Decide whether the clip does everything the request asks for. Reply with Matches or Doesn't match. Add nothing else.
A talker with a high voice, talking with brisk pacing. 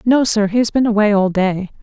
Matches